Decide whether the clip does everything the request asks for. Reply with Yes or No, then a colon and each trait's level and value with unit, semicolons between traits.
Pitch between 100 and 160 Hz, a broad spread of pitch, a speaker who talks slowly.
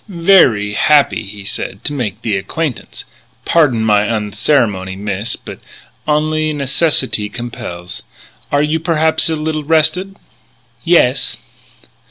Yes: low, 135 Hz; wide, 7.0 semitones; slow, 115 wpm